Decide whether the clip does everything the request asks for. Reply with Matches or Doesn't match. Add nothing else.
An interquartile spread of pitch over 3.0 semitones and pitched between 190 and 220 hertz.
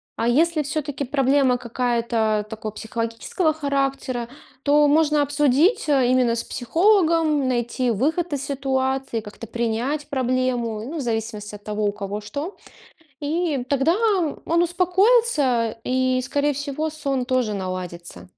Doesn't match